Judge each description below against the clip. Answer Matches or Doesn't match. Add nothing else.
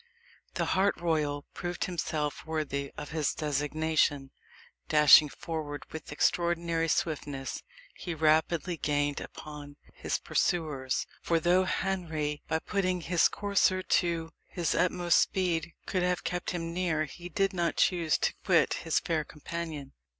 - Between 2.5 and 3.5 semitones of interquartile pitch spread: Matches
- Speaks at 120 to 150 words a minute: Matches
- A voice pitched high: Doesn't match